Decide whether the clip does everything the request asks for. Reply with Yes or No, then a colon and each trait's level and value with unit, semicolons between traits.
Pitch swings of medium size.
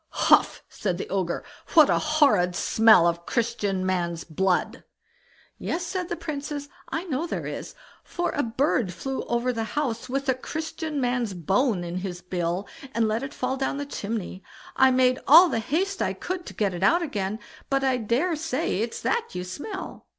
No: wide, 7.7 semitones